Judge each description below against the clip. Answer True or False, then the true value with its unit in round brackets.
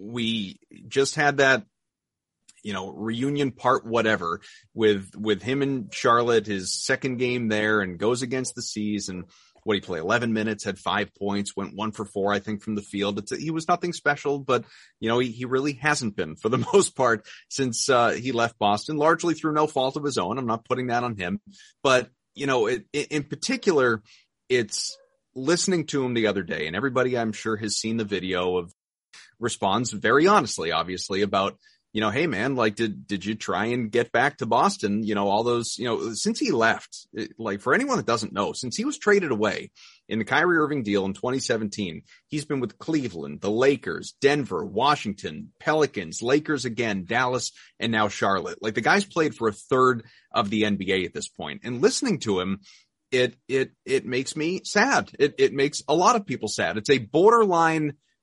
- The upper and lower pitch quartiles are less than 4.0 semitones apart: False (5.3 semitones)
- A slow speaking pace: False (200 wpm)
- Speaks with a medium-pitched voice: False (120 Hz)